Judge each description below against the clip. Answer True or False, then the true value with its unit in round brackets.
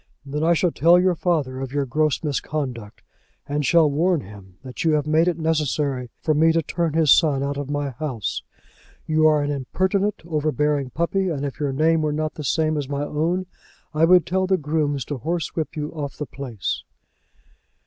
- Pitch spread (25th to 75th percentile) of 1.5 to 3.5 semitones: True (2.6 semitones)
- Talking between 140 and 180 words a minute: False (195 wpm)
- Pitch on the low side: False (150 Hz)